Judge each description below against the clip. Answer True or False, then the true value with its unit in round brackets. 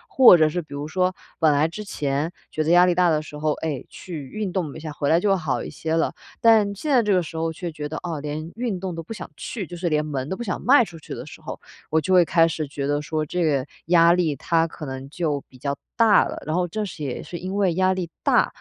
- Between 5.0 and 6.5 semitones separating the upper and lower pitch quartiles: False (3.4 semitones)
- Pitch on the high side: False (165 Hz)